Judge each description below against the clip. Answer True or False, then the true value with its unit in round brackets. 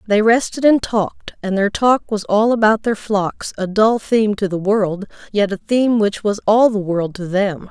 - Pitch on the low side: False (210 Hz)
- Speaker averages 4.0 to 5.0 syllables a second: True (4.6 syllables/s)